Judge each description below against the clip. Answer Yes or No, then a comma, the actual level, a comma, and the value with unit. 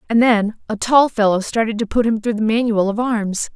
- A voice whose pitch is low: No, high, 220 Hz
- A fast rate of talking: Yes, fast, 235 wpm